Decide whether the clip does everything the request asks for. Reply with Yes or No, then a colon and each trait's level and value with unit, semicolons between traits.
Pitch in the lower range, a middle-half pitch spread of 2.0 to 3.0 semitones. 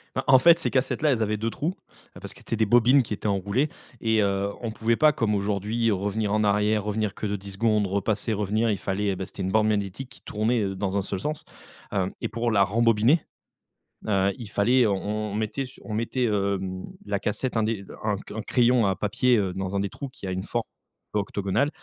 Yes: low, 105 Hz; average, 2.7 semitones